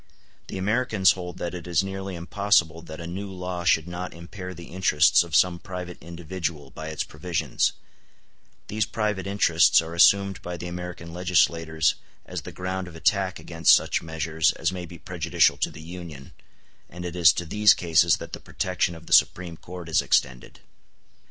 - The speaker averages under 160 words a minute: No, average, 175 wpm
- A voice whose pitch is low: Yes, very low, 85 Hz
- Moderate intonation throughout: No, narrow, 2.0 semitones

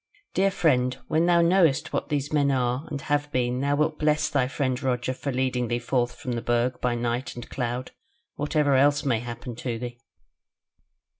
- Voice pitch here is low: Yes, low, 130 Hz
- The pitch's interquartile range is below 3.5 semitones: Yes, average, 3.1 semitones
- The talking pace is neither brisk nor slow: Yes, average, 190 wpm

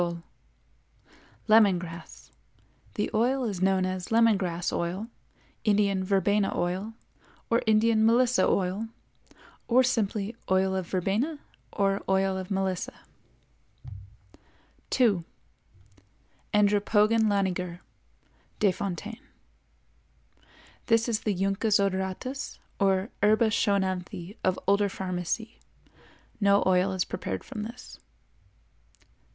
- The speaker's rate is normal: No, slow, 95 wpm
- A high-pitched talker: Yes, high, 200 Hz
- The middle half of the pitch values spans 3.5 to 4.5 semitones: No, average, 2.7 semitones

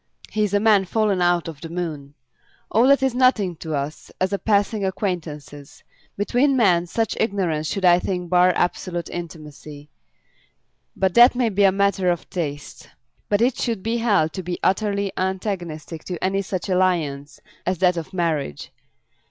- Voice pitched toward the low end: No, medium, 185 Hz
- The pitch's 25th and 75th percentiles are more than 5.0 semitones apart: No, average, 3.6 semitones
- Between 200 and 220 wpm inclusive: No, average, 165 wpm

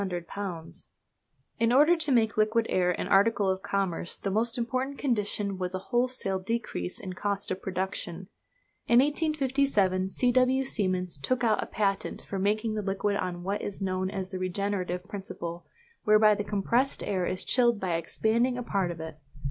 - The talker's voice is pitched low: No, high, 205 Hz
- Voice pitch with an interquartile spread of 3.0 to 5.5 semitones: Yes, average, 4.1 semitones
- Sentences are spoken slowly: No, average, 170 wpm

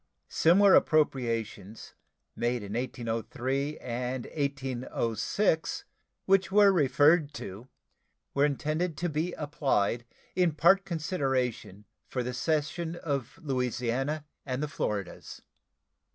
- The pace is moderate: No, slow, 100 wpm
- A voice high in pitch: No, medium, 140 Hz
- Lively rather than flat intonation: No, average, 4.6 semitones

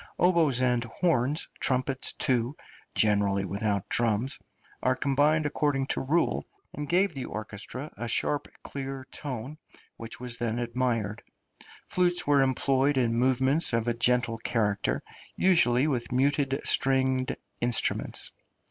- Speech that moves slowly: Yes, slow, 125 wpm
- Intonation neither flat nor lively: Yes, average, 3.3 semitones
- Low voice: Yes, low, 130 Hz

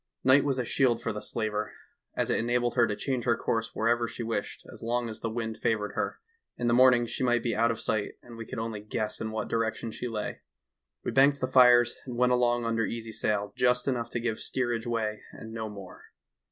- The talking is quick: Yes, fast, 235 wpm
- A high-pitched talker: No, low, 115 Hz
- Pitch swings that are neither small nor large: No, narrow, 1.7 semitones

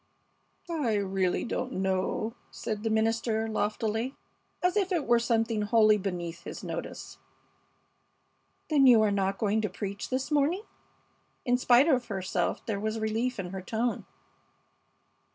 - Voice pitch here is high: Yes, high, 220 Hz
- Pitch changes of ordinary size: Yes, average, 3.6 semitones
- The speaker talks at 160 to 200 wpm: No, average, 140 wpm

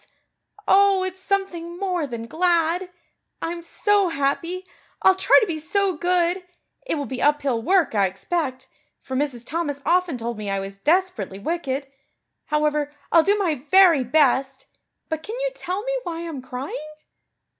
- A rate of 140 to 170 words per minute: Yes, average, 155 wpm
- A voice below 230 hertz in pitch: No, very high, 330 Hz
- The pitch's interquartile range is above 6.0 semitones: No, average, 5.2 semitones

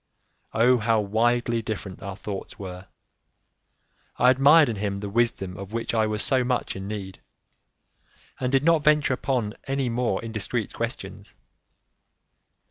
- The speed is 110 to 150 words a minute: Yes, average, 140 wpm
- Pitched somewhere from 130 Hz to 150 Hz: No, low, 115 Hz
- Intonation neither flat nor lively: Yes, average, 3.8 semitones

